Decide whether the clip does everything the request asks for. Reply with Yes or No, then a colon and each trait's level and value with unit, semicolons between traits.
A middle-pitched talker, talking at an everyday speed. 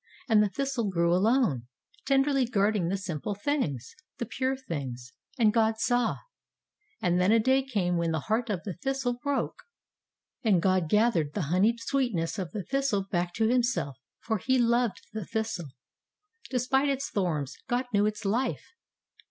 No: high, 215 Hz; average, 170 wpm